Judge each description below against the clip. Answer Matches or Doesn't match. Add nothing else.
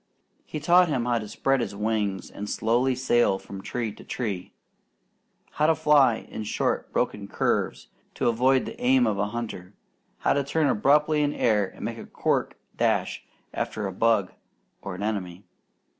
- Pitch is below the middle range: Matches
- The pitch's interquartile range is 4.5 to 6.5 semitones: Matches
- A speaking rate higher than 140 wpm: Matches